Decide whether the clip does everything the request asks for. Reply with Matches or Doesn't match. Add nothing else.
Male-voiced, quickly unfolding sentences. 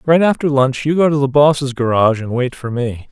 Matches